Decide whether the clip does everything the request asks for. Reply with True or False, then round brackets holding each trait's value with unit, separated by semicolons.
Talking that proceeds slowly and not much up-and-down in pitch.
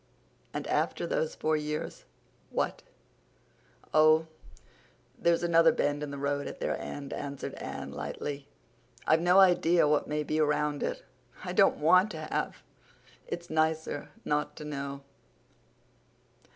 True (125 wpm; 2.2 semitones)